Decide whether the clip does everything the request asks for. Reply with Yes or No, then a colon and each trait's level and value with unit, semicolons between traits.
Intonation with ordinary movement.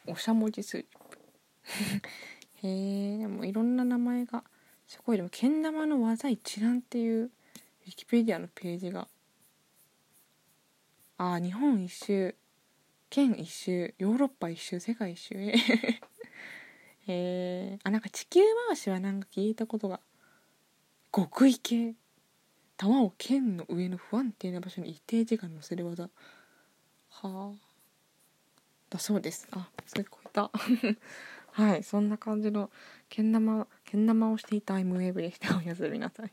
Yes: average, 3.8 semitones